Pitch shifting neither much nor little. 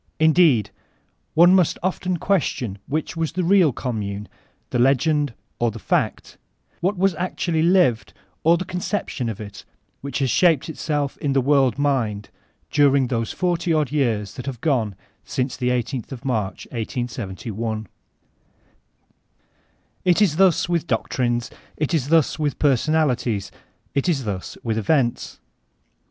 No: wide, 5.7 semitones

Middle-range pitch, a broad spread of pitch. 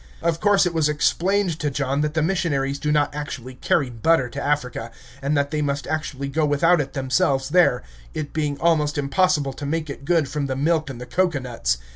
No: medium, 145 Hz; average, 2.8 semitones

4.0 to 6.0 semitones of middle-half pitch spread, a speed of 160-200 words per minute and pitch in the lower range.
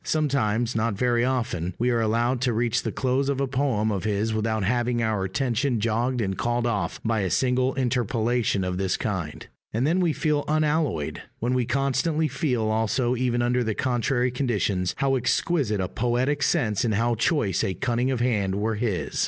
No: average, 3.2 semitones; average, 185 wpm; low, 120 Hz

